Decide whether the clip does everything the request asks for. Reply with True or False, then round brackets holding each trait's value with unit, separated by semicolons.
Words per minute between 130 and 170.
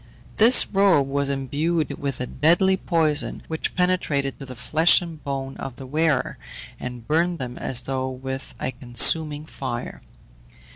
True (150 wpm)